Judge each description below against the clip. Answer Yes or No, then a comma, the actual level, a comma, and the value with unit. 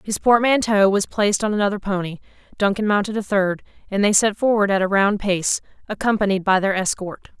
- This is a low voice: No, high, 200 Hz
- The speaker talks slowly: No, average, 185 wpm